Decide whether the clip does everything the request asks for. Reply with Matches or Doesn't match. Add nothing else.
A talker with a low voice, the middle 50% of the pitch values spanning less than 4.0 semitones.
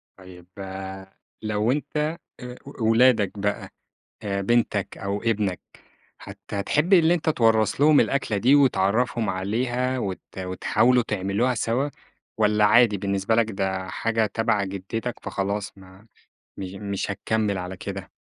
Matches